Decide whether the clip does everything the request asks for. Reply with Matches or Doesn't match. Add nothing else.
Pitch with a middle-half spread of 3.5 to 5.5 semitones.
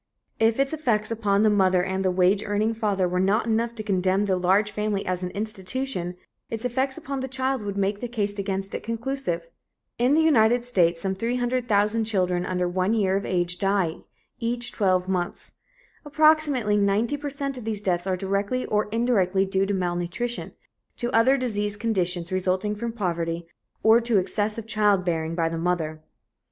Matches